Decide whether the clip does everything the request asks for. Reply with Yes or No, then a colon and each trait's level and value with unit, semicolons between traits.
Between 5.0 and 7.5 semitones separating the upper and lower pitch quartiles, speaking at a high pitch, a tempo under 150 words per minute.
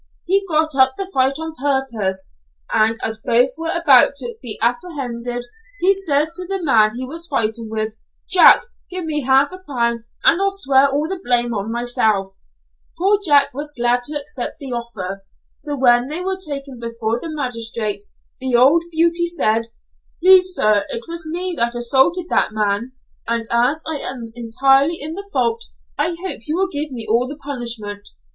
No: wide, 5.6 semitones; very high, 270 Hz; average, 180 wpm